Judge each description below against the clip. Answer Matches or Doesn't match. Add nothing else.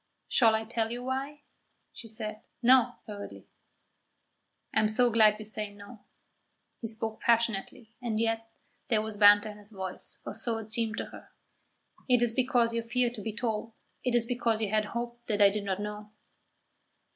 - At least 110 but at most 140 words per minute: Doesn't match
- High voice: Matches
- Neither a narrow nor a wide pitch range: Doesn't match